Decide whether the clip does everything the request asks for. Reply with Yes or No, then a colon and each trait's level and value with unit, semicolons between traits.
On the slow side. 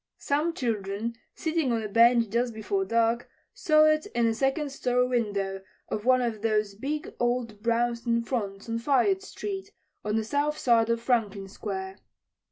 No: average, 165 wpm